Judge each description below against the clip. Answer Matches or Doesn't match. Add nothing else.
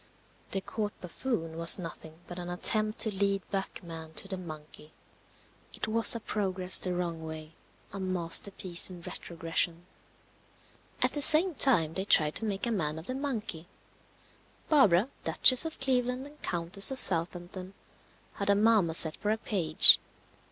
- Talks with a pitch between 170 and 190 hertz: Matches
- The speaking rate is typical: Matches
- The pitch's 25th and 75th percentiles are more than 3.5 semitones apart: Matches